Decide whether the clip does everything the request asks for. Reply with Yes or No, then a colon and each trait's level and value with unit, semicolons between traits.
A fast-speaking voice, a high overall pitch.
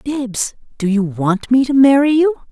No: average, 190 wpm; very high, 250 Hz